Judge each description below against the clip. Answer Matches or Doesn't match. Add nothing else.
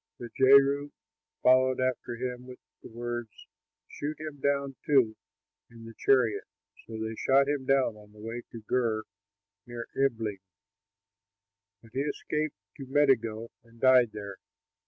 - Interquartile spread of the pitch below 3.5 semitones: Matches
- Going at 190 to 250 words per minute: Doesn't match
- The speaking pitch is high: Doesn't match